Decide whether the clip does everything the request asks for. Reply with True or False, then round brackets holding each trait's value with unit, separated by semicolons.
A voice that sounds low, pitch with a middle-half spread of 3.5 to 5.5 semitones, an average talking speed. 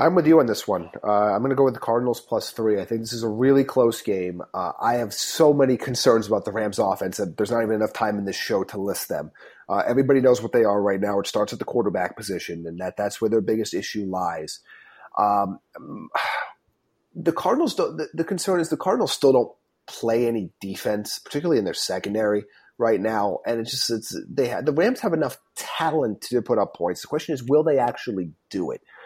False (115 Hz; 4.4 semitones; 230 wpm)